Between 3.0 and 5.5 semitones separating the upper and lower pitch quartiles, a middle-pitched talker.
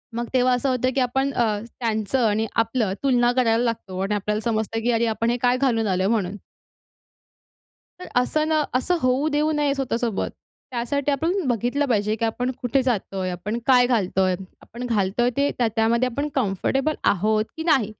No: average, 3.4 semitones; high, 240 Hz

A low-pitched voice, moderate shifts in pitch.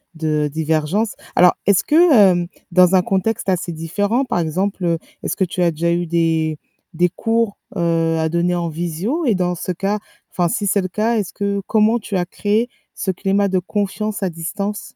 No: medium, 185 Hz; average, 3.5 semitones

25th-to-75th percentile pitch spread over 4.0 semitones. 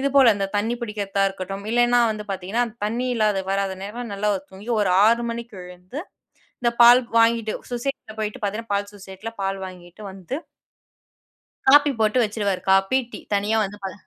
No: average, 3.3 semitones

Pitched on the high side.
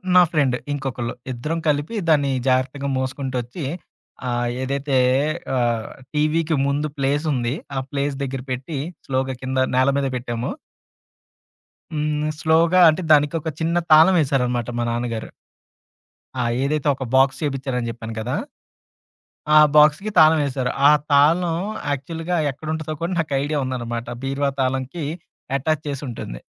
No: medium, 140 Hz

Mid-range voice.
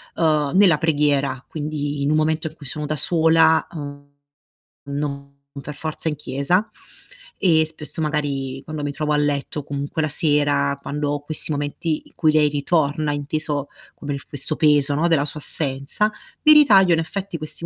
Yes: medium, 150 Hz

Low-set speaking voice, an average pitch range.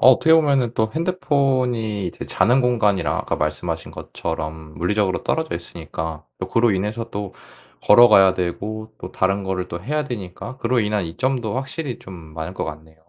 No: low, 105 Hz; wide, 6.1 semitones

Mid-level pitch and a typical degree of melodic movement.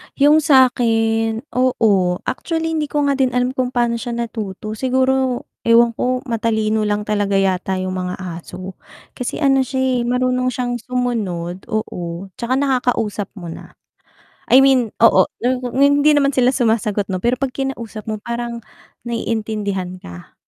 No: high, 235 Hz; average, 3.6 semitones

